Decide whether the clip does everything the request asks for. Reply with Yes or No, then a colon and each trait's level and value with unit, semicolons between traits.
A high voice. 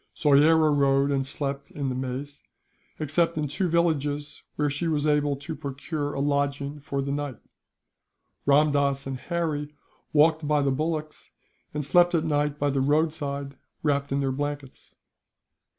No: medium, 145 Hz